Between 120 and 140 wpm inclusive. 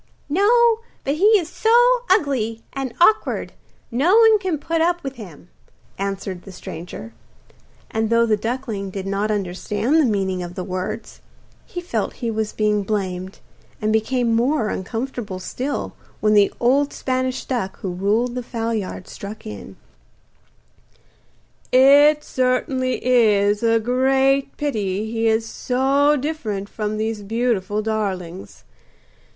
Yes: slow, 135 wpm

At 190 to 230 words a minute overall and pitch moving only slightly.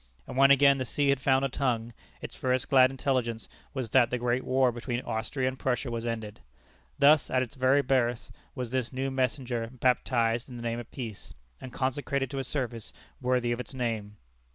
Yes: average, 200 wpm; narrow, 2.0 semitones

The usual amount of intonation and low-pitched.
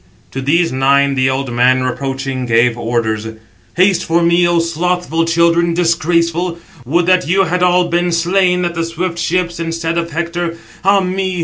No: average, 4.3 semitones; medium, 170 Hz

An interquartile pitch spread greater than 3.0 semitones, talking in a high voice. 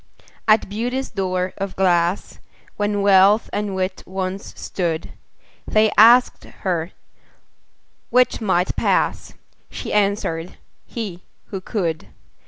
No: narrow, 2.4 semitones; high, 195 Hz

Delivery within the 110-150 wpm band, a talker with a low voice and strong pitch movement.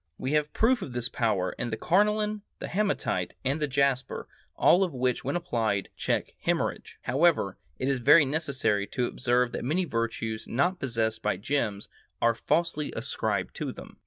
No: average, 170 wpm; low, 130 Hz; wide, 6.3 semitones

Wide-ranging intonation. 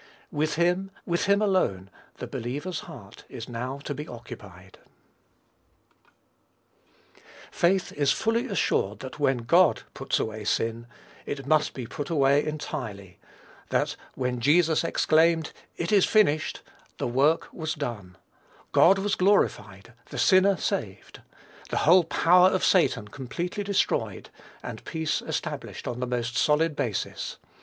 Yes: wide, 6.6 semitones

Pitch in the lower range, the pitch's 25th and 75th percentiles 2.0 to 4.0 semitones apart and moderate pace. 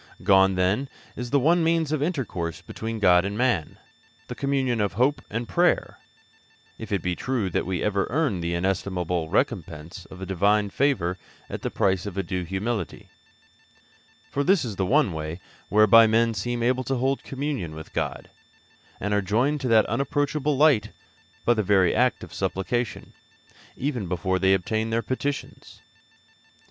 No: low, 105 Hz; wide, 5.6 semitones; average, 165 wpm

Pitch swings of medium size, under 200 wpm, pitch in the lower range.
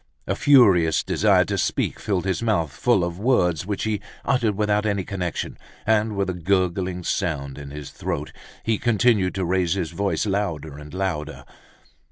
Yes: average, 3.8 semitones; average, 170 wpm; very low, 95 Hz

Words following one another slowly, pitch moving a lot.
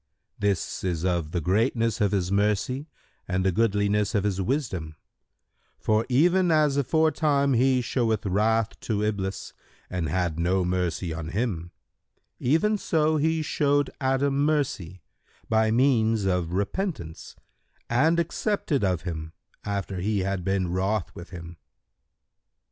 Yes: slow, 130 wpm; wide, 7.0 semitones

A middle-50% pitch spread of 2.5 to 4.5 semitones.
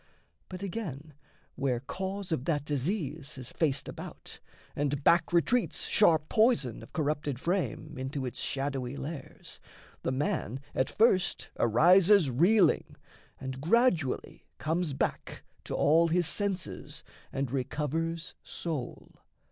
No: average, 4.9 semitones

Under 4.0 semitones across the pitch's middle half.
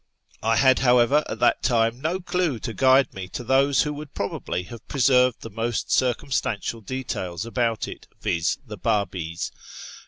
Yes: average, 3.5 semitones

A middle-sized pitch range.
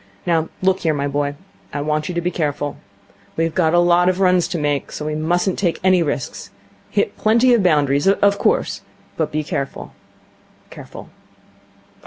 Yes: average, 3.7 semitones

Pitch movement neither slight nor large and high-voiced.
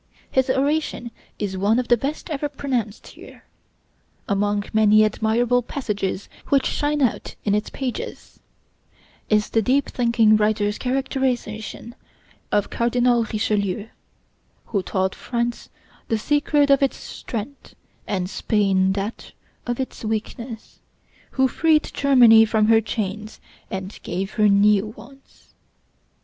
Yes: average, 3.8 semitones; high, 225 Hz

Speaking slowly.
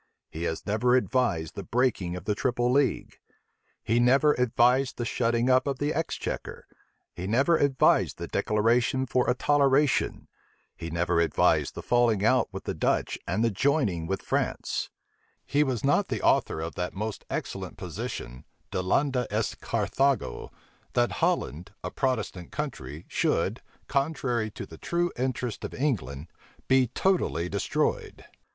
No: average, 145 wpm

